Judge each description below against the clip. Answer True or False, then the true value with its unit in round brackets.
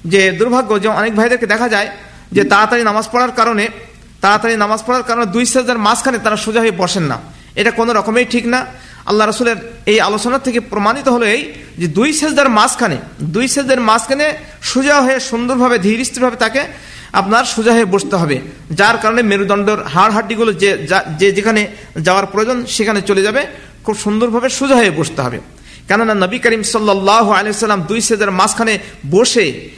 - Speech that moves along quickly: True (150 wpm)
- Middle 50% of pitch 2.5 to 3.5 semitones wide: True (3.0 semitones)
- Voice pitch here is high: True (220 Hz)